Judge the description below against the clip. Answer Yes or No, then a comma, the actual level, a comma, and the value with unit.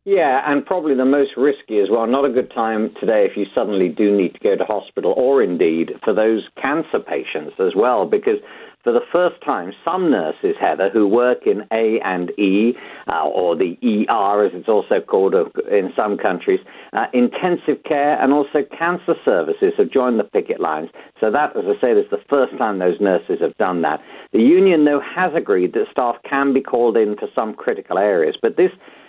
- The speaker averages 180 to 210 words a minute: Yes, average, 200 wpm